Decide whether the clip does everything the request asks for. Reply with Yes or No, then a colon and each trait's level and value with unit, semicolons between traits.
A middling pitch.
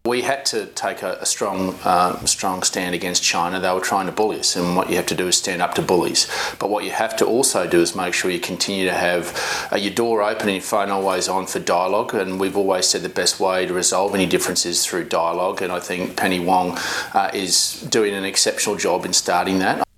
No: very low, 95 Hz